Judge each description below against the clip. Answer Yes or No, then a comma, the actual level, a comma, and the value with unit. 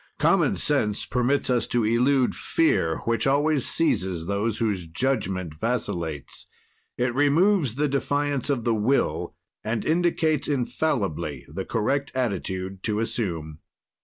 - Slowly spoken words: Yes, slow, 125 wpm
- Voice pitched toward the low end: Yes, low, 120 Hz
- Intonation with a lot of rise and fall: Yes, wide, 6.3 semitones